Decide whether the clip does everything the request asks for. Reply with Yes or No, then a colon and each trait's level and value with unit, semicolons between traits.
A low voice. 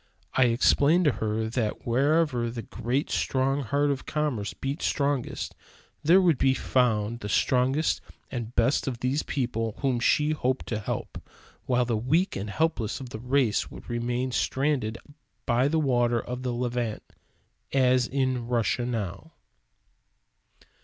Yes: low, 125 Hz